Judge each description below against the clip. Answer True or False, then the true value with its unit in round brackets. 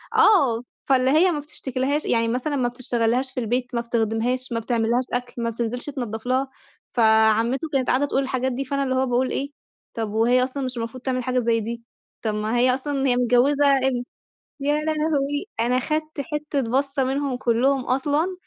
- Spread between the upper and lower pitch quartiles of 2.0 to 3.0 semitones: True (2.7 semitones)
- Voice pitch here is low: False (255 Hz)